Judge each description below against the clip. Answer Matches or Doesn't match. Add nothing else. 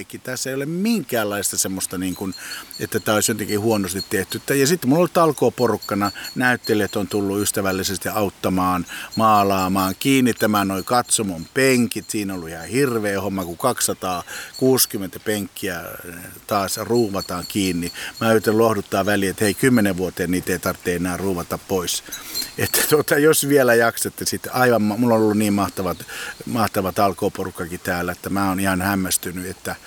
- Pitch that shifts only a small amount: Doesn't match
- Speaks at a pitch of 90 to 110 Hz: Matches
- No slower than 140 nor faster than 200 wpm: Matches